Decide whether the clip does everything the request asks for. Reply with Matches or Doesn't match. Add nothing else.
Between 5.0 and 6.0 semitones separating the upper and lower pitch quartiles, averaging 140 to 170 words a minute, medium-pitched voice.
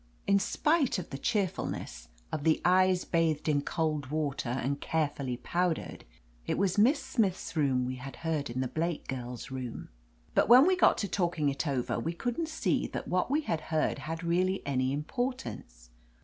Doesn't match